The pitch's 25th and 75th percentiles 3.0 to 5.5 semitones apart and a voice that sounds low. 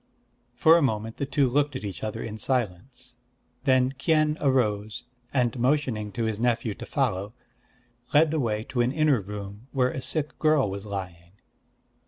Yes: average, 4.7 semitones; low, 120 Hz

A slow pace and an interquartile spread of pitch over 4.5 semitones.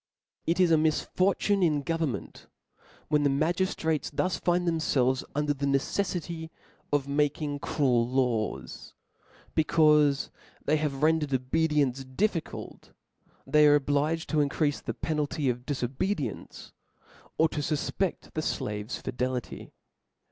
No: slow, 125 wpm; average, 2.9 semitones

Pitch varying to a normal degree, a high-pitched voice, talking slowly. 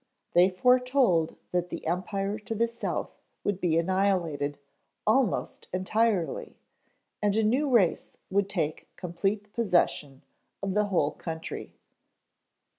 Yes: average, 3.8 semitones; high, 195 Hz; slow, 115 wpm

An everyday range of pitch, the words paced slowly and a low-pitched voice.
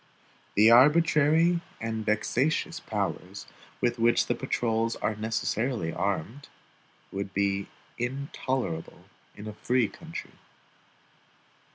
Yes: average, 3.9 semitones; slow, 95 wpm; low, 115 Hz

